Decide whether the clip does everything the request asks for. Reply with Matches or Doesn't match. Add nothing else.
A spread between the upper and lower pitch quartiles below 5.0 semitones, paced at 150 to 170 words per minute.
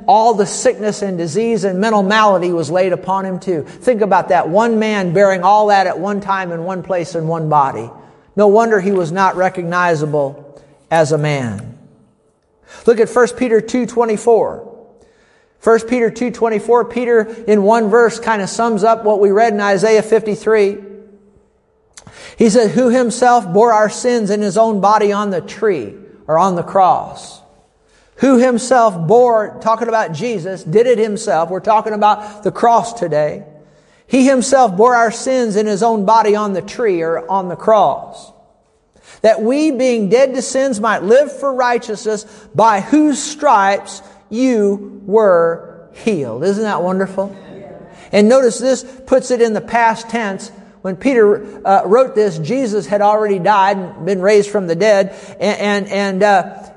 Matches